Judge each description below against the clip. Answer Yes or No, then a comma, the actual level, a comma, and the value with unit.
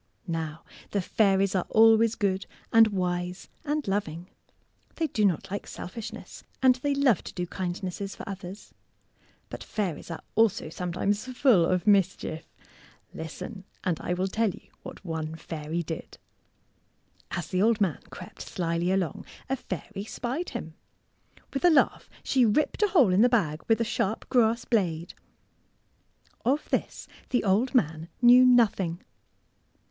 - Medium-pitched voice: No, high, 195 Hz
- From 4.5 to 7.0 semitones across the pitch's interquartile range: Yes, average, 4.8 semitones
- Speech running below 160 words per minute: Yes, average, 150 wpm